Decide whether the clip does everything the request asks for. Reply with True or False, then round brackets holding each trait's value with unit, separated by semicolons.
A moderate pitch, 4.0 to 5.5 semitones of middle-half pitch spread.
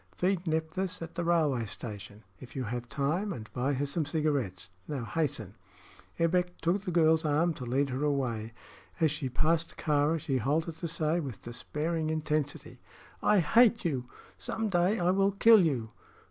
True (155 Hz; 4.6 semitones)